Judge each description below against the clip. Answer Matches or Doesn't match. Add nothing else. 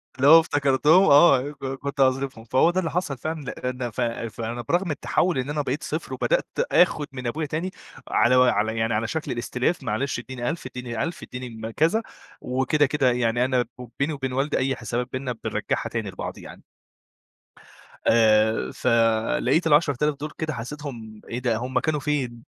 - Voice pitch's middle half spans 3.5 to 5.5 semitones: Matches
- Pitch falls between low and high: Doesn't match